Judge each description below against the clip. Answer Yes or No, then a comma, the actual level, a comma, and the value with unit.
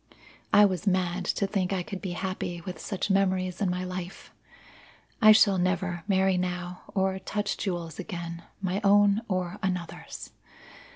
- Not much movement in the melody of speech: Yes, narrow, 1.6 semitones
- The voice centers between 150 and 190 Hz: Yes, medium, 185 Hz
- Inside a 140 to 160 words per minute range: Yes, average, 155 wpm